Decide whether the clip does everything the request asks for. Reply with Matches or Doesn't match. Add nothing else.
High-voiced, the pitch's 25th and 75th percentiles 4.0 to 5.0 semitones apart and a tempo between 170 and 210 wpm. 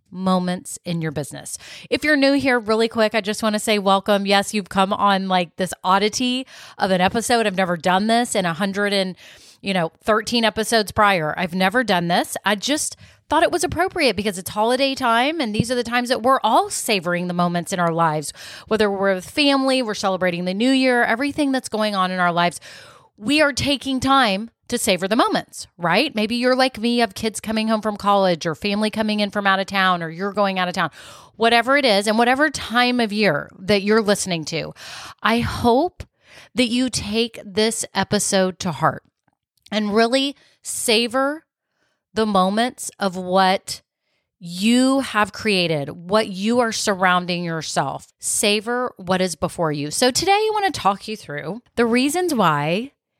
Matches